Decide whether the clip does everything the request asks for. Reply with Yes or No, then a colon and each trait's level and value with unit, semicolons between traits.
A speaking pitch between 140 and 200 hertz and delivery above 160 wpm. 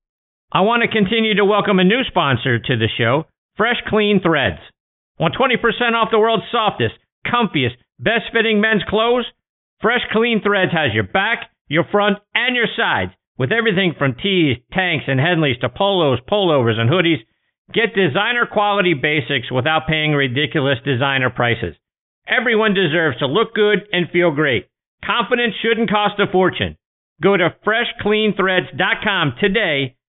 No: medium, 185 Hz; average, 150 wpm